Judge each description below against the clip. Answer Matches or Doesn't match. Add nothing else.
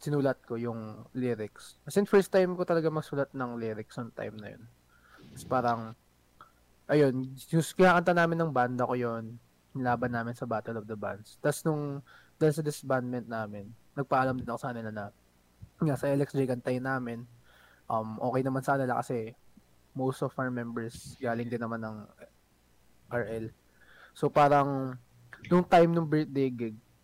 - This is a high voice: Doesn't match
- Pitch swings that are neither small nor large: Matches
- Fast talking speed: Matches